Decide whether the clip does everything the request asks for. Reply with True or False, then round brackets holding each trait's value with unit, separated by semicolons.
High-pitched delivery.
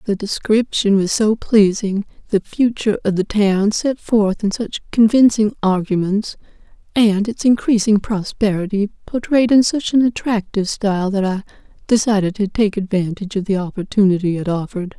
True (205 Hz)